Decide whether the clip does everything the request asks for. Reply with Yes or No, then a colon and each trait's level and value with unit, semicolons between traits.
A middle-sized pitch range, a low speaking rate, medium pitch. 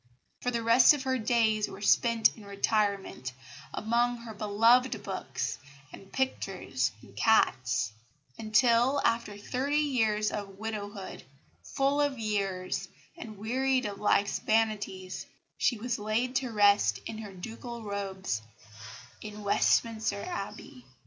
No: average, 3.1 semitones; slow, 120 wpm; high, 220 Hz